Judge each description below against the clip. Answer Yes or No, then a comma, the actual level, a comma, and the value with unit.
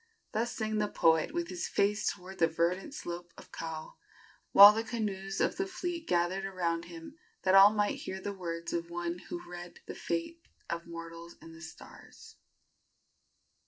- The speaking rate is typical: Yes, average, 170 wpm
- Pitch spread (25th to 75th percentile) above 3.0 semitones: Yes, average, 3.9 semitones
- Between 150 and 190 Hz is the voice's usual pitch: Yes, medium, 185 Hz